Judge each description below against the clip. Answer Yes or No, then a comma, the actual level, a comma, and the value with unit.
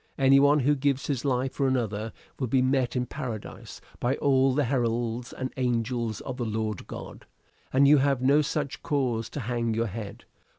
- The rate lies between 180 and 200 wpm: Yes, average, 185 wpm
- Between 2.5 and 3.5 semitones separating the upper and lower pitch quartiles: Yes, average, 2.9 semitones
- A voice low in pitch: Yes, low, 130 Hz